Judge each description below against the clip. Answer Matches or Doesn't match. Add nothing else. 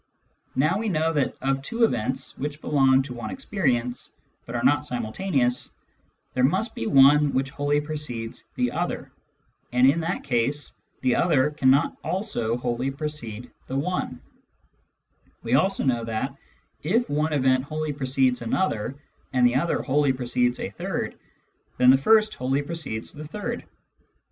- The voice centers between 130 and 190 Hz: Matches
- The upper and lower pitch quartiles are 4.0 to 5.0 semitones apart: Doesn't match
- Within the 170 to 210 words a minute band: Doesn't match